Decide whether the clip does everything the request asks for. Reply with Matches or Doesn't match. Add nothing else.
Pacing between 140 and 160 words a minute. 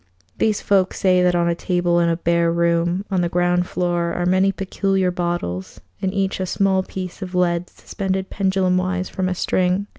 Doesn't match